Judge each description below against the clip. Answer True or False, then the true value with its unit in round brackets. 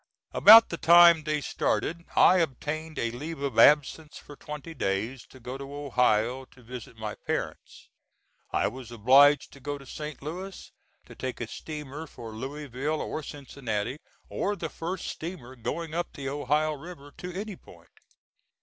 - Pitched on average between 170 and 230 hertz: False (145 Hz)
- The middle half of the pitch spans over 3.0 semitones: True (4.0 semitones)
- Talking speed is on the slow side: False (160 wpm)